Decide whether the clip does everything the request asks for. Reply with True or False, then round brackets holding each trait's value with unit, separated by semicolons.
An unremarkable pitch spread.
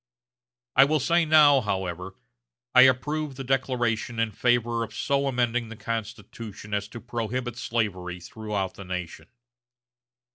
True (3.8 semitones)